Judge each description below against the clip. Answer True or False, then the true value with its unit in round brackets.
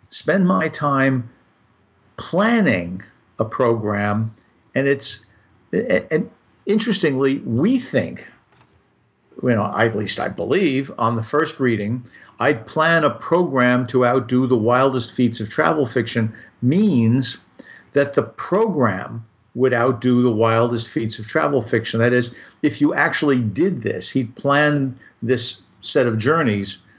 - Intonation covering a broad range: False (4.0 semitones)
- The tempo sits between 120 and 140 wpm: True (135 wpm)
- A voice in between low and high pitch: False (125 Hz)